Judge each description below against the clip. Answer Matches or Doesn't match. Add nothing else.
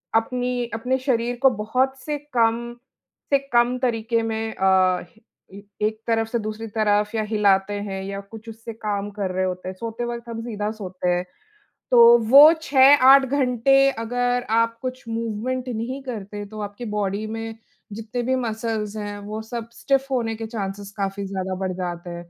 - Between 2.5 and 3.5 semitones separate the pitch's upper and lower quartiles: Matches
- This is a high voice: Matches